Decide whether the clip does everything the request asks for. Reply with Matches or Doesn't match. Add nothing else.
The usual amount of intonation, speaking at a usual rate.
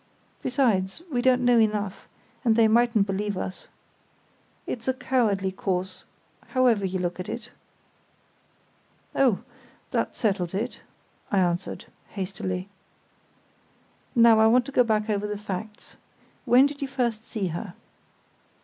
Doesn't match